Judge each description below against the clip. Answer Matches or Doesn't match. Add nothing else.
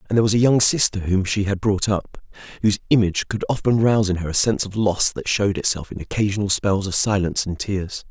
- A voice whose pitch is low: Matches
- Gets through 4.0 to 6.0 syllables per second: Doesn't match